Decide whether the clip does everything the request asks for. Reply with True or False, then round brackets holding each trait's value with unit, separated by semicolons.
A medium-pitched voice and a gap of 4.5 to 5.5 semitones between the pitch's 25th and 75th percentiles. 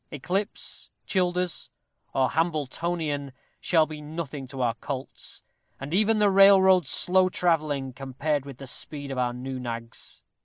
True (150 Hz; 5.0 semitones)